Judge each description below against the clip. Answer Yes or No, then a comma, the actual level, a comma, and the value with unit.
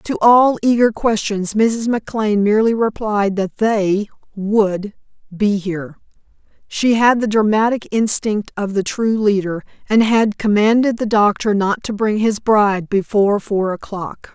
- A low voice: No, high, 210 Hz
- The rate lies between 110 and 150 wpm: Yes, average, 145 wpm